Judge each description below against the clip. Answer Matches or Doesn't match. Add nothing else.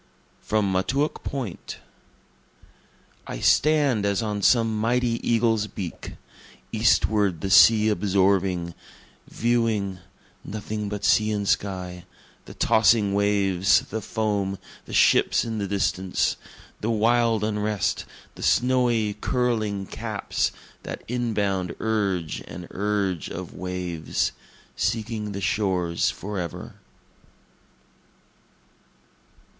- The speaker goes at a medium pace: Doesn't match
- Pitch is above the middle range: Doesn't match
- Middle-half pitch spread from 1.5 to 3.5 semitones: Matches